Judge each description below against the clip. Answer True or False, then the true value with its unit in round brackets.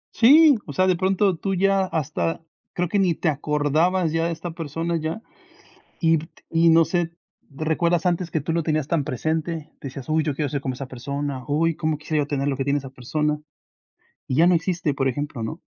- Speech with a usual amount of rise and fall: True (3.0 semitones)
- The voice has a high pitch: False (160 Hz)